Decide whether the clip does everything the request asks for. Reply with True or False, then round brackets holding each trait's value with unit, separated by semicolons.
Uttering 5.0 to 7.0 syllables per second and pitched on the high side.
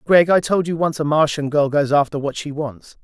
False (5.2 syllables/s; 150 Hz)